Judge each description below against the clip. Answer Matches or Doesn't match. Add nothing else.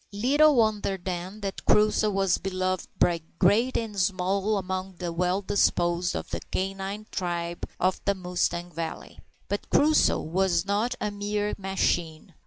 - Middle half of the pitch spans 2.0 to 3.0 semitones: Matches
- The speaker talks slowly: Doesn't match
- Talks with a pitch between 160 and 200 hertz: Matches